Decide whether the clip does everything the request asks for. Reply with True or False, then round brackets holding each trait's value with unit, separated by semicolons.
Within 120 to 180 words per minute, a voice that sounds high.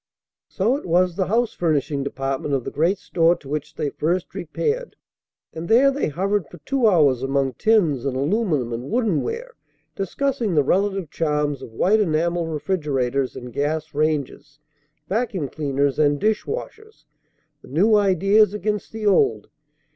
False (155 wpm; 170 Hz)